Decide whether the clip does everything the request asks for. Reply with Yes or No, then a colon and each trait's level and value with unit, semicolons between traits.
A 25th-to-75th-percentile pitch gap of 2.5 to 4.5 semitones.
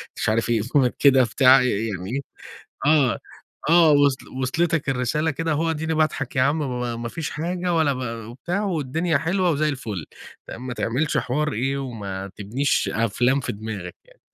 No: average, 5.0 semitones